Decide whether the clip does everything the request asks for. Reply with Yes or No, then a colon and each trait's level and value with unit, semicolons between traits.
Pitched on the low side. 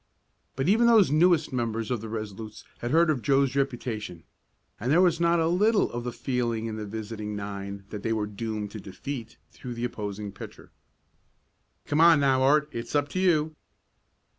Yes: low, 120 Hz